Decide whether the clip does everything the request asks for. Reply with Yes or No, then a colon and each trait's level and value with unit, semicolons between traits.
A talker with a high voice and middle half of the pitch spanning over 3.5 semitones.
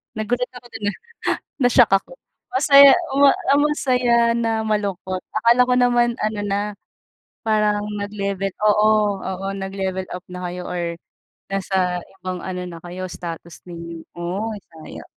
Yes: high, 205 Hz; average, 4.3 semitones